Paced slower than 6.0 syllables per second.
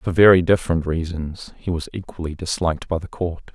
Yes: 5.5 syllables/s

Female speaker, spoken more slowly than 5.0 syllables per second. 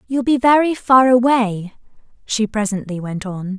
Yes: female; 4.5 syllables/s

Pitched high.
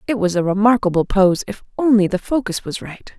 Yes: high, 205 Hz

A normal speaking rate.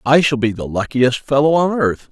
No: fast, 225 wpm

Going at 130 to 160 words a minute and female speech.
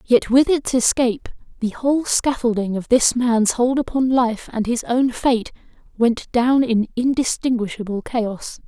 Yes: average, 150 wpm; female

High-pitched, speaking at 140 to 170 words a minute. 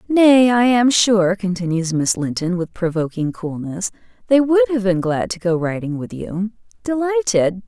Yes: high, 200 Hz; average, 165 wpm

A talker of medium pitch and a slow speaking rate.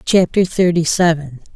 Yes: medium, 170 Hz; slow, 115 wpm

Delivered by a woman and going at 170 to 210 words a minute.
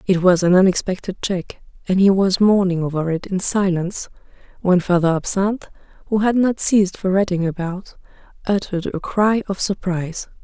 No: female; average, 155 wpm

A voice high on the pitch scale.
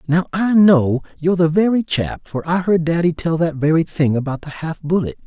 No: medium, 165 Hz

